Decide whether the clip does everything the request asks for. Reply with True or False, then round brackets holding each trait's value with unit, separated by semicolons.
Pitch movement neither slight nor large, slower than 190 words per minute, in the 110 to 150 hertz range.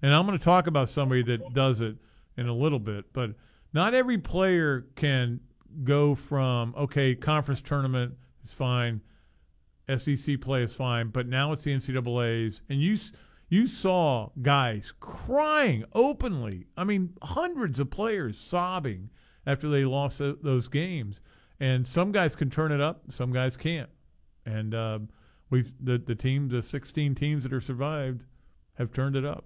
True (3.8 semitones; 160 wpm; 135 Hz)